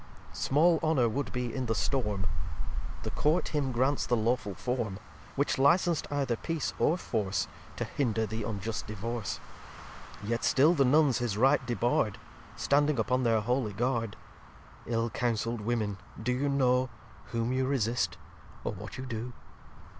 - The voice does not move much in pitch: No, average, 3.5 semitones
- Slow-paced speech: No, average, 155 wpm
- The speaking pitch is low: Yes, low, 120 Hz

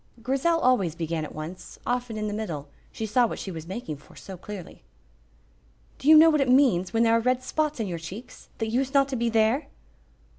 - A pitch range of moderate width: No, wide, 6.1 semitones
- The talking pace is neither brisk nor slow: No, fast, 220 wpm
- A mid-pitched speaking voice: No, high, 225 Hz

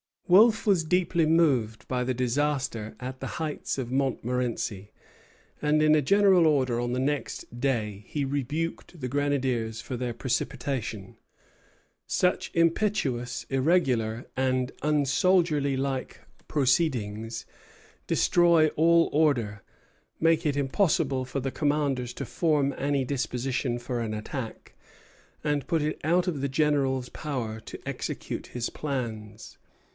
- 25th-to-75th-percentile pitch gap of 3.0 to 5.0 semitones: Yes, average, 3.9 semitones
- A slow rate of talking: Yes, slow, 125 wpm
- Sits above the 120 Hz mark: Yes, low, 135 Hz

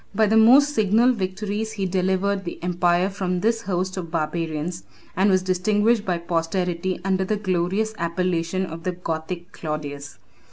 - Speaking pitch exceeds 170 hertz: Yes, medium, 185 Hz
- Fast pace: No, average, 155 wpm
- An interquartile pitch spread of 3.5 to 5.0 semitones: No, average, 3.0 semitones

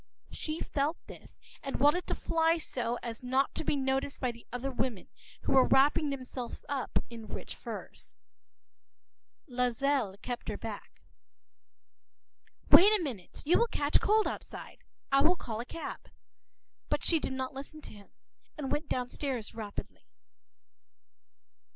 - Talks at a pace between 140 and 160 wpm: Yes, average, 145 wpm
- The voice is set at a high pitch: Yes, very high, 270 Hz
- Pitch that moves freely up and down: No, average, 3.4 semitones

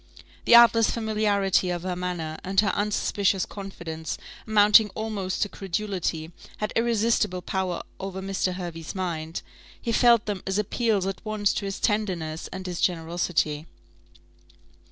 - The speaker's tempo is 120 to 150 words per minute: Yes, slow, 135 wpm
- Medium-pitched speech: No, high, 195 Hz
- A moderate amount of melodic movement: Yes, average, 3.1 semitones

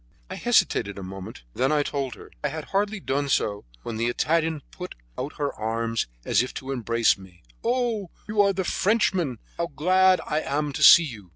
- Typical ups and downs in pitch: No, wide, 7.8 semitones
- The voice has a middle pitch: Yes, medium, 145 Hz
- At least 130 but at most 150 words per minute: No, average, 200 wpm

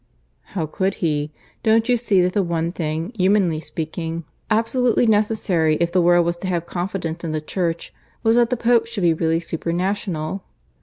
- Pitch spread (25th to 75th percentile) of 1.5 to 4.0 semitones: No, average, 4.4 semitones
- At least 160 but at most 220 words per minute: Yes, average, 185 wpm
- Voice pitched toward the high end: No, medium, 175 Hz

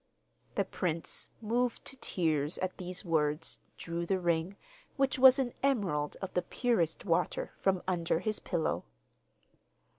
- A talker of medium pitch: Yes, medium, 180 Hz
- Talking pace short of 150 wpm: Yes, average, 140 wpm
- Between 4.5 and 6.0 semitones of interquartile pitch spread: Yes, average, 5.0 semitones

